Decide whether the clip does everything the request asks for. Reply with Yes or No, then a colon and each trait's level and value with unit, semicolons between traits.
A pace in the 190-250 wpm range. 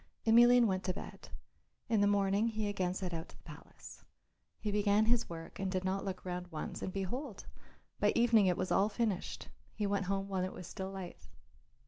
Yes: average, 200 wpm